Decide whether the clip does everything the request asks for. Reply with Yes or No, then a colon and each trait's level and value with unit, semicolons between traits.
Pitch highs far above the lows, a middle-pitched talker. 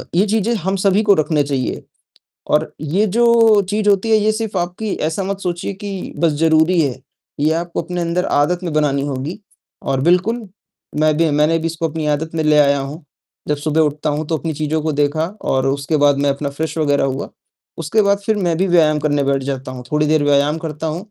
No: average, 3.7 semitones; medium, 160 Hz